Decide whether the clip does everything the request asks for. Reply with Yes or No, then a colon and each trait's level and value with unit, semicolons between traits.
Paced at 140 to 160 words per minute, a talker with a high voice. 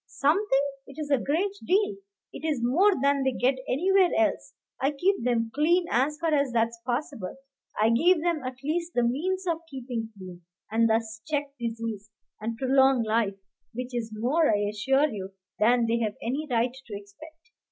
No: average, 175 wpm; very high, 265 Hz